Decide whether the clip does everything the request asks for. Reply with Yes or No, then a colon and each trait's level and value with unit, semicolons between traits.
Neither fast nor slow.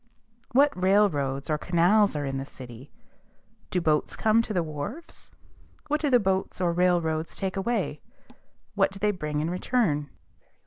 Yes: average, 160 wpm